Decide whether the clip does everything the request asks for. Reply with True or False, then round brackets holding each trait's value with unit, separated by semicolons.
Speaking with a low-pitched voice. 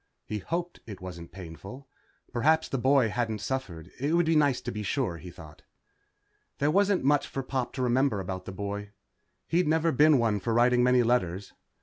True (125 Hz)